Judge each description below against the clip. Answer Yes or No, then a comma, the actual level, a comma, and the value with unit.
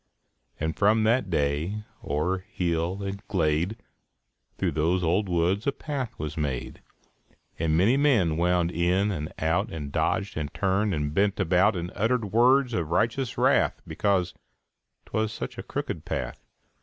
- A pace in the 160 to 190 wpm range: No, average, 150 wpm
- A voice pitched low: Yes, very low, 95 Hz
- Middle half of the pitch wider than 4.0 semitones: Yes, average, 4.6 semitones